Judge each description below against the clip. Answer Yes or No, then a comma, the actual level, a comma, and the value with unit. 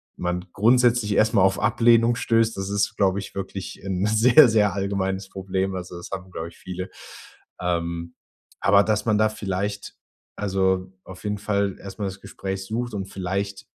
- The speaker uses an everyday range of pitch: No, narrow, 2.1 semitones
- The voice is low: Yes, low, 100 Hz